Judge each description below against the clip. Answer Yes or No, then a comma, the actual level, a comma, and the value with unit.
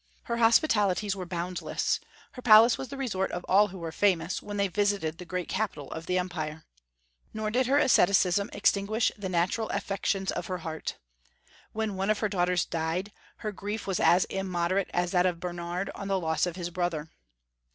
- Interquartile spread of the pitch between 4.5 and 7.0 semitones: No, average, 2.9 semitones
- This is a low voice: No, high, 190 Hz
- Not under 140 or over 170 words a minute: No, average, 185 wpm